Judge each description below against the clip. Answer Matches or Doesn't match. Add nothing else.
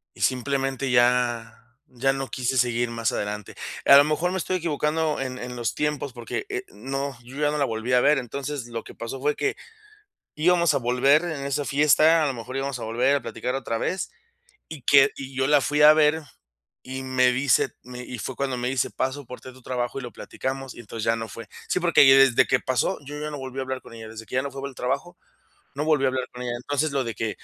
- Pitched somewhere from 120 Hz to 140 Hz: Matches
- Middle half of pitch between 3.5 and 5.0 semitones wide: Doesn't match